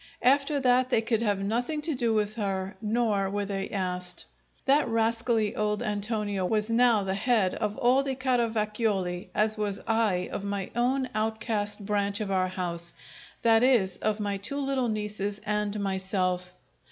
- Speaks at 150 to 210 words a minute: Yes, average, 165 wpm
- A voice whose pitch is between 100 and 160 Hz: No, high, 210 Hz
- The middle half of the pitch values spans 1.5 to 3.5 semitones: Yes, average, 2.9 semitones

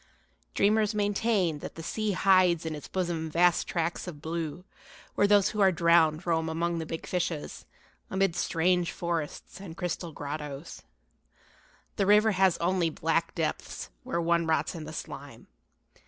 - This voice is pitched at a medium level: Yes, medium, 170 Hz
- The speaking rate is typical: Yes, average, 155 wpm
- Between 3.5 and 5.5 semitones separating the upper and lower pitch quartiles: No, average, 2.8 semitones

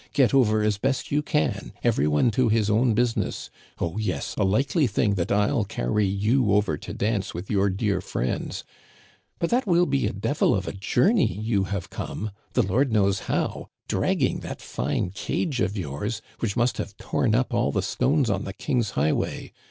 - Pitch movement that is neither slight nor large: Yes, average, 4.3 semitones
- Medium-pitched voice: No, low, 105 Hz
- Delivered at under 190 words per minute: No, average, 195 wpm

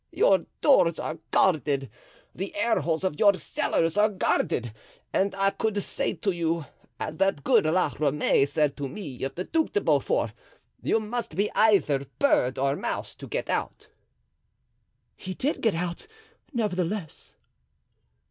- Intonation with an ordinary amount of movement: No, wide, 5.8 semitones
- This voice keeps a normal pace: Yes, average, 150 wpm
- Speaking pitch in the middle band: Yes, medium, 180 Hz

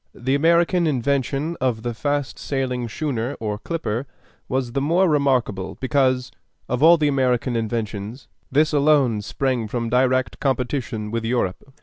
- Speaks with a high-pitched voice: No, low, 130 Hz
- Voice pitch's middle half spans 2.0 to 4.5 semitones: Yes, average, 3.4 semitones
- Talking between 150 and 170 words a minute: No, slow, 135 wpm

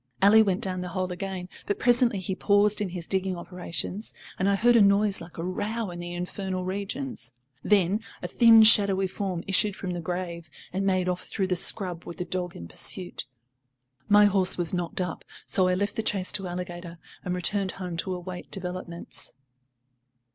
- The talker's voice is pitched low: No, medium, 185 Hz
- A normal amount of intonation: No, narrow, 2.2 semitones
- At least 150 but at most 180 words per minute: No, average, 190 wpm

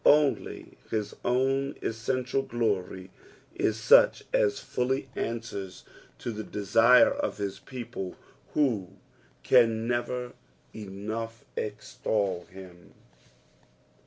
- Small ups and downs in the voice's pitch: No, average, 4.1 semitones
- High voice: No, low, 115 Hz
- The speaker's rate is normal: No, slow, 95 wpm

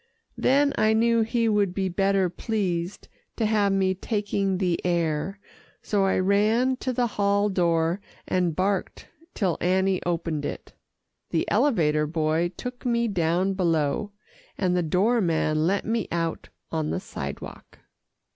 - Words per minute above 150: No, average, 145 wpm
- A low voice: No, high, 190 Hz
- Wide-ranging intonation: No, average, 3.7 semitones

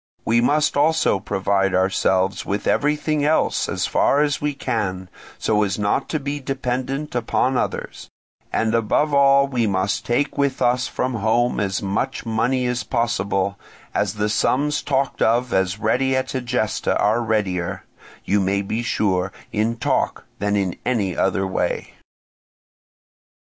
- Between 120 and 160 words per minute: Yes, average, 150 wpm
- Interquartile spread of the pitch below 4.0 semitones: No, average, 5.0 semitones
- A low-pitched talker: Yes, low, 115 Hz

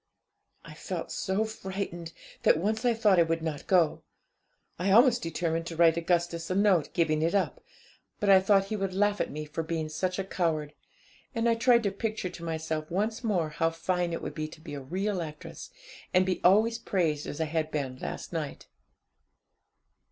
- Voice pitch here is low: No, medium, 175 Hz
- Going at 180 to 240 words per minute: Yes, average, 195 wpm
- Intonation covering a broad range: No, average, 3.9 semitones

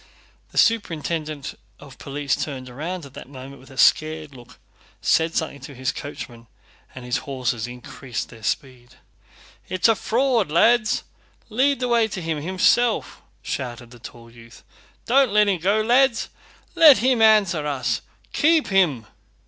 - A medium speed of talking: Yes, average, 150 wpm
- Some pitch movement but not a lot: No, wide, 9.0 semitones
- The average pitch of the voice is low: No, medium, 155 Hz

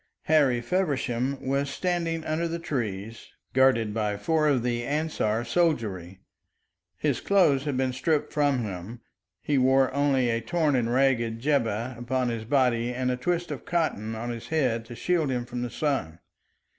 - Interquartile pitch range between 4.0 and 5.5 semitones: Yes, average, 4.3 semitones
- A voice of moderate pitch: No, low, 130 Hz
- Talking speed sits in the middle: Yes, average, 165 wpm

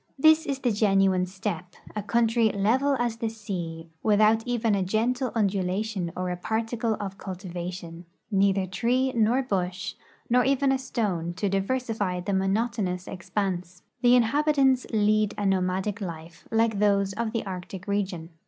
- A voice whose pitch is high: Yes, high, 205 Hz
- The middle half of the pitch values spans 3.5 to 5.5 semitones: Yes, average, 3.9 semitones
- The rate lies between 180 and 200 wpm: No, average, 155 wpm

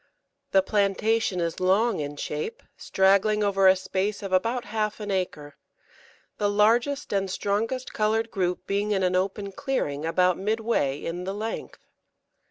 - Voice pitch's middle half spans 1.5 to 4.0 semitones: Yes, average, 2.8 semitones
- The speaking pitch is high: Yes, high, 200 Hz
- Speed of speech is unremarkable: Yes, average, 150 wpm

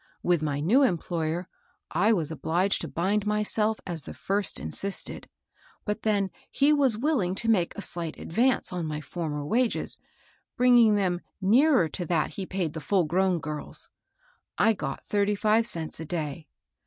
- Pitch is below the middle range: No, high, 190 Hz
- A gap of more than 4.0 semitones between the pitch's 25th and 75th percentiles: Yes, average, 4.7 semitones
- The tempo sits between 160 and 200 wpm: Yes, average, 165 wpm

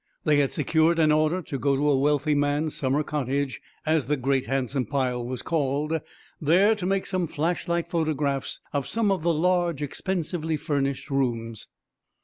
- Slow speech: No, average, 165 wpm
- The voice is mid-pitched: Yes, medium, 150 Hz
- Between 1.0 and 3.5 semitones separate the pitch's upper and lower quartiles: Yes, average, 3.2 semitones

